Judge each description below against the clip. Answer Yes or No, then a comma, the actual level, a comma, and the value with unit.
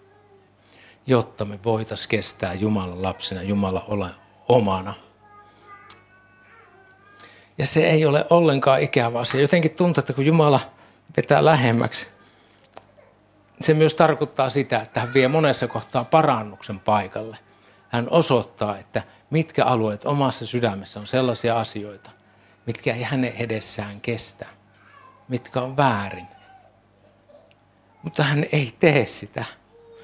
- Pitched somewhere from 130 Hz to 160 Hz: No, low, 120 Hz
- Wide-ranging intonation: Yes, wide, 6.1 semitones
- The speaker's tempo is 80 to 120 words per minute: Yes, average, 115 wpm